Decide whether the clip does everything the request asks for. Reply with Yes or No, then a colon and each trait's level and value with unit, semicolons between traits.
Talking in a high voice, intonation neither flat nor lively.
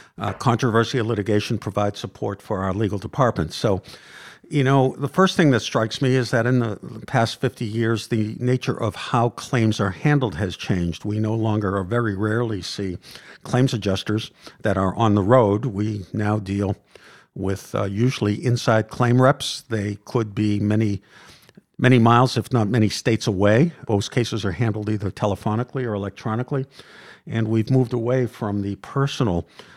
No: low, 110 Hz; average, 3.3 semitones